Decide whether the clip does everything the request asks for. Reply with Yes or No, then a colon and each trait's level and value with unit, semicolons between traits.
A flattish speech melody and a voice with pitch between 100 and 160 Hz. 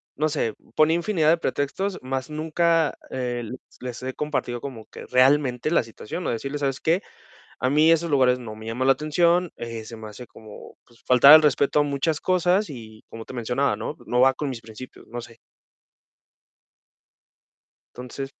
No: average, 4.2 semitones; low, 135 Hz